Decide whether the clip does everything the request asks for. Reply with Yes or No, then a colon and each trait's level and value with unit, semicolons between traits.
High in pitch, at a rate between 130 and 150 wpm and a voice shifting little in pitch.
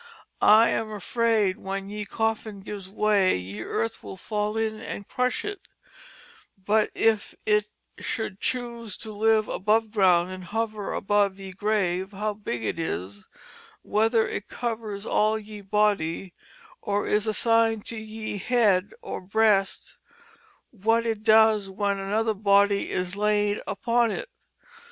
Yes: high, 210 Hz; average, 140 wpm; narrow, 2.2 semitones